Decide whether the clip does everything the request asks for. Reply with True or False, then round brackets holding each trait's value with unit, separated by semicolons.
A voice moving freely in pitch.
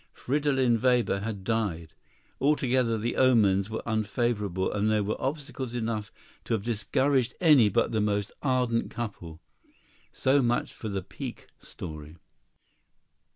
False (3.9 semitones)